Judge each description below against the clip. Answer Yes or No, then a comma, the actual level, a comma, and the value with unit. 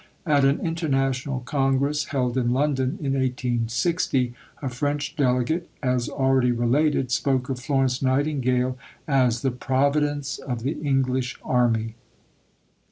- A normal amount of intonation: No, narrow, 2.2 semitones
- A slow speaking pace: Yes, slow, 120 wpm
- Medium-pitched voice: No, low, 130 Hz